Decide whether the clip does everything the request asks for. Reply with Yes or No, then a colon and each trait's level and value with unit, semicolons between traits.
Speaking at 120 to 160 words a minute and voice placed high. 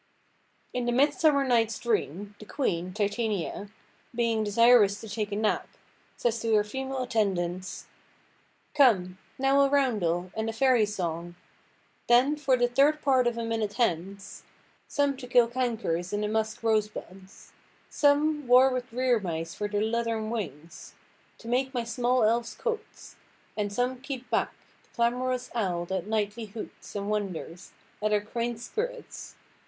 Yes: average, 150 wpm; high, 230 Hz